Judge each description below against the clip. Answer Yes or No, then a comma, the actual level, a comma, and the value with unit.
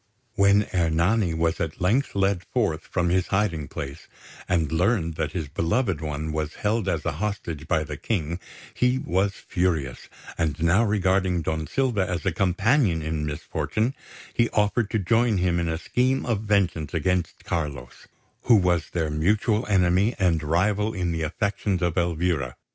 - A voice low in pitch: Yes, very low, 90 Hz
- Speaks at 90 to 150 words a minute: No, average, 165 wpm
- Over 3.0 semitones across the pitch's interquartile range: Yes, average, 4.2 semitones